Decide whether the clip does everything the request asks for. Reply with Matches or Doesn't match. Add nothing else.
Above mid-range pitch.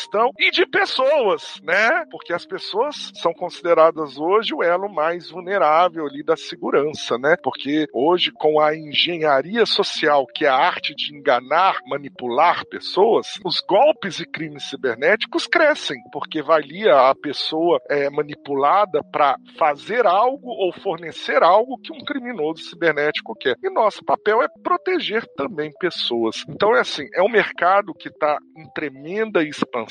Doesn't match